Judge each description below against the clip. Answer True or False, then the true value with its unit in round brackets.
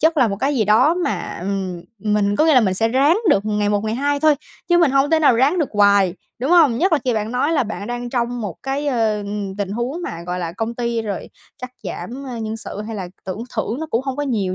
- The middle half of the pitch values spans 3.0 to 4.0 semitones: False (5.2 semitones)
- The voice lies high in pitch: True (230 Hz)